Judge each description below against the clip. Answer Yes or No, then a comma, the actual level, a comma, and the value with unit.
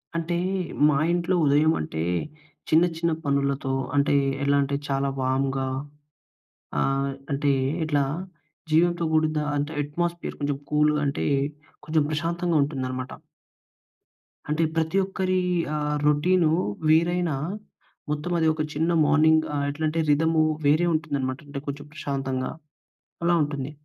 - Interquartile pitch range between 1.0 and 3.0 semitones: Yes, narrow, 2.5 semitones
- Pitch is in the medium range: Yes, medium, 150 Hz